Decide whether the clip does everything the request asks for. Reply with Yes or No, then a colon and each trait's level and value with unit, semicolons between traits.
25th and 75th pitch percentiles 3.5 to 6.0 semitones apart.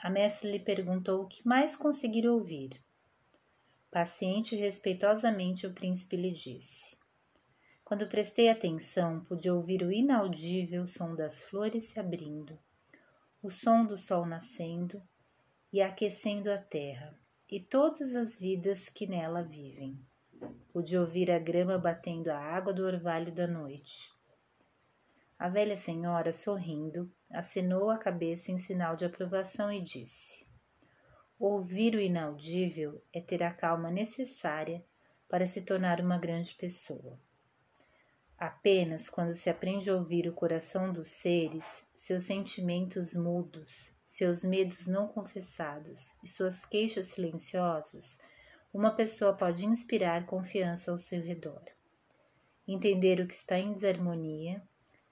No: average, 2.8 semitones